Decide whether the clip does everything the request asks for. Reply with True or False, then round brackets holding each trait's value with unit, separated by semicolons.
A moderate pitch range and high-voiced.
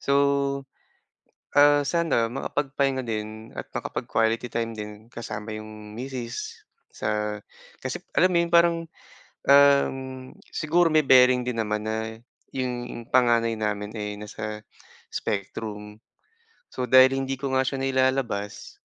False (4.1 semitones; 120 Hz)